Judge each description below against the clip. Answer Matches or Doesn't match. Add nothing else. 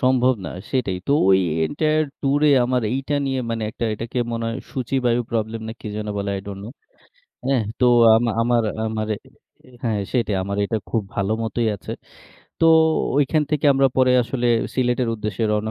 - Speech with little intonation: Doesn't match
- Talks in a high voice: Doesn't match